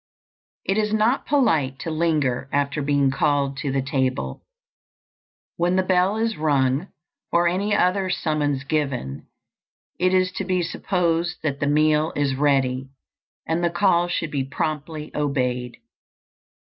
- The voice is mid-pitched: Yes, medium, 155 Hz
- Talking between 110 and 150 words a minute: Yes, average, 140 wpm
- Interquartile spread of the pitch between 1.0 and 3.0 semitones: No, average, 4.5 semitones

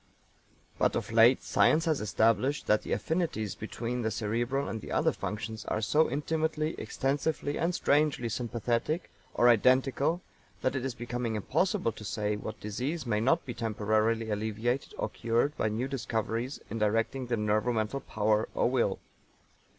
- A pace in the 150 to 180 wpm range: Yes, average, 155 wpm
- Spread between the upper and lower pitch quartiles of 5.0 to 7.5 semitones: No, average, 3.9 semitones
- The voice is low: Yes, low, 120 Hz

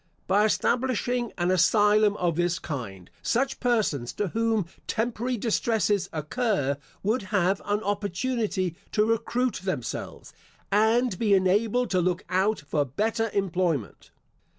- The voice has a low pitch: No, high, 205 Hz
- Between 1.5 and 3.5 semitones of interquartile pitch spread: No, average, 4.2 semitones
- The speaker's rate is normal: No, slow, 125 wpm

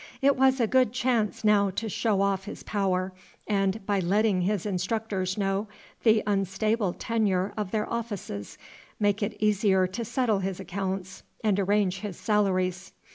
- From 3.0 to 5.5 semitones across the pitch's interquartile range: No, narrow, 2.4 semitones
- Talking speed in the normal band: Yes, average, 155 wpm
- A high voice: Yes, high, 200 Hz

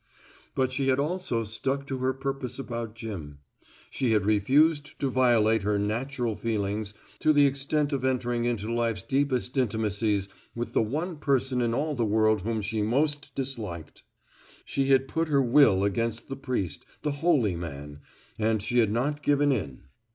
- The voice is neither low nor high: No, low, 120 Hz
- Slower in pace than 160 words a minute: No, average, 165 wpm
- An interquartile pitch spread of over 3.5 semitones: Yes, average, 4.2 semitones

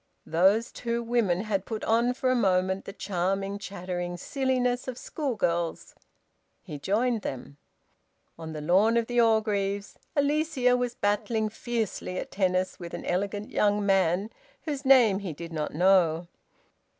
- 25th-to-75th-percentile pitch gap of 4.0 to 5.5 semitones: Yes, average, 4.5 semitones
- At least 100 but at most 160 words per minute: Yes, average, 145 wpm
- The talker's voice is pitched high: Yes, high, 205 Hz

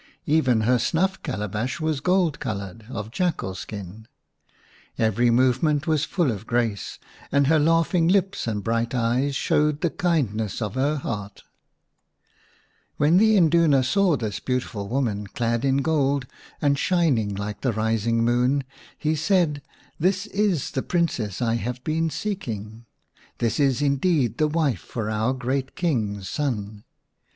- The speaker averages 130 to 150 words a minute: Yes, average, 145 wpm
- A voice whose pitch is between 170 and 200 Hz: No, low, 130 Hz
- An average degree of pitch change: No, wide, 6.0 semitones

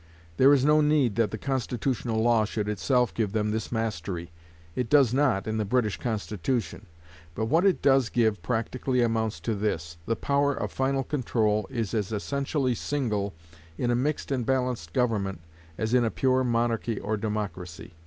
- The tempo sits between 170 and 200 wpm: Yes, average, 175 wpm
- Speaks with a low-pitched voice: Yes, low, 115 Hz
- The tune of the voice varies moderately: Yes, average, 3.5 semitones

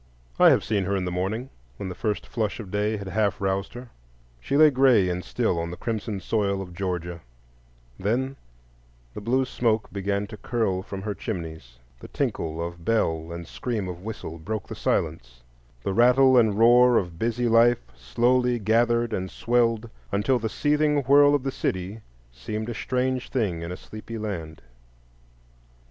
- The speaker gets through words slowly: No, average, 175 wpm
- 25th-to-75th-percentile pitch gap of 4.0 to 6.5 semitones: Yes, average, 4.8 semitones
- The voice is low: Yes, low, 105 Hz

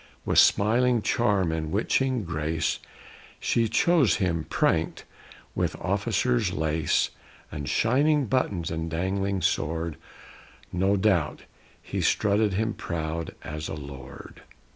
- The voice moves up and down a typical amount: No, wide, 5.7 semitones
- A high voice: No, very low, 95 Hz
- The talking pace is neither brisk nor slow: No, slow, 115 wpm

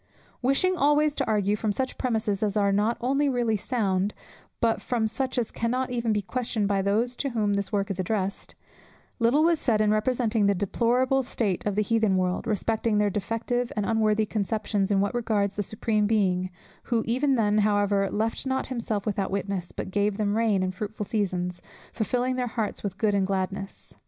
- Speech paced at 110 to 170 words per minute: No, average, 190 wpm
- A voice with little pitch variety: No, average, 3.0 semitones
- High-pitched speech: Yes, high, 215 Hz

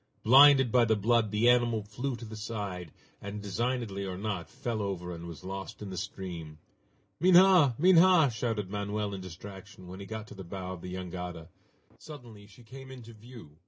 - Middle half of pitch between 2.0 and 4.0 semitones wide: No, average, 4.4 semitones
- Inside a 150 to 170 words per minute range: No, average, 185 wpm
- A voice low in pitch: Yes, low, 105 Hz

